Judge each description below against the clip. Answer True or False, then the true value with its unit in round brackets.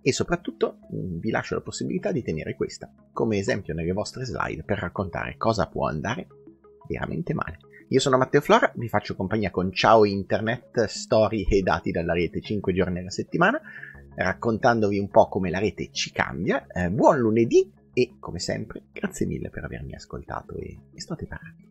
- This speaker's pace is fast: True (175 wpm)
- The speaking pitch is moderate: False (105 Hz)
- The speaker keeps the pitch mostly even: False (4.3 semitones)